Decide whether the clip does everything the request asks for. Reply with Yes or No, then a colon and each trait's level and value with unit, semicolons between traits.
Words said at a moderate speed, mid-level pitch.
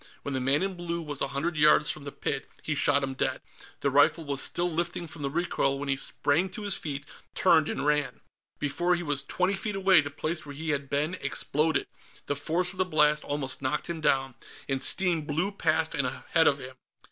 No: fast, 220 wpm; medium, 150 Hz